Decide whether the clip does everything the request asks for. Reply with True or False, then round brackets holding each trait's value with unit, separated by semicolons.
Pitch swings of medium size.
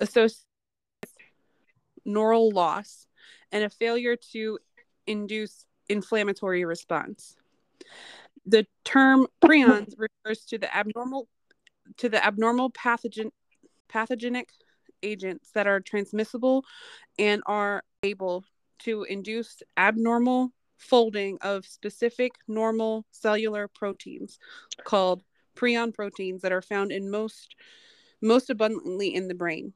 True (3.2 semitones)